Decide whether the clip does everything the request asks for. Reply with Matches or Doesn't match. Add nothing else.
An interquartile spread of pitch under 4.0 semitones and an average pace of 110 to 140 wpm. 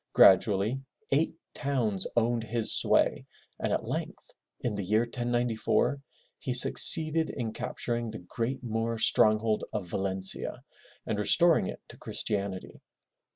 Matches